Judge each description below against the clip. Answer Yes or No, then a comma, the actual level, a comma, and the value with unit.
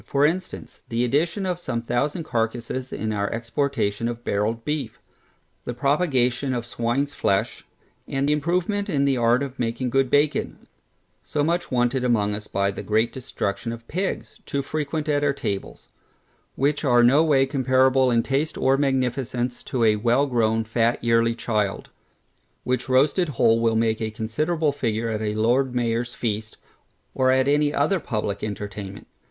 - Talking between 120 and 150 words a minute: No, average, 160 wpm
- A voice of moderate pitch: No, low, 125 Hz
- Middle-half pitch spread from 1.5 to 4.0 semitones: Yes, average, 3.7 semitones